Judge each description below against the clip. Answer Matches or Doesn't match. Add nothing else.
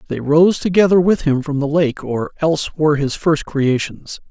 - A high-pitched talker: Doesn't match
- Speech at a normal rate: Matches